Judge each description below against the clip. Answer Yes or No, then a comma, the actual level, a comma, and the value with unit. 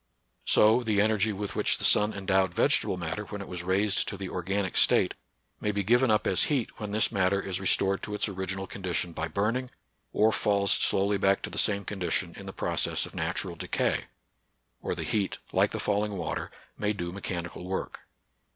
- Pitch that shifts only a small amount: Yes, narrow, 2.0 semitones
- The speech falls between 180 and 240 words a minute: Yes, average, 200 wpm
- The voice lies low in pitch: Yes, low, 100 Hz